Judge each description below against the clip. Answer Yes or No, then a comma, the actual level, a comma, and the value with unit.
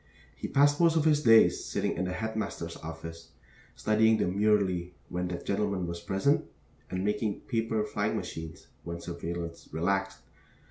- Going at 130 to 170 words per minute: Yes, average, 145 wpm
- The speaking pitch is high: No, very low, 95 Hz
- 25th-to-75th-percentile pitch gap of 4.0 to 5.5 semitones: Yes, average, 4.4 semitones